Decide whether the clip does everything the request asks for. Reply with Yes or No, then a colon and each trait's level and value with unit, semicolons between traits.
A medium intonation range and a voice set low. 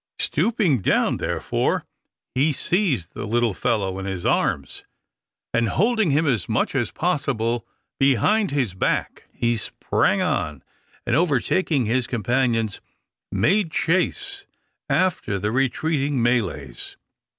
No: wide, 6.8 semitones; low, 130 Hz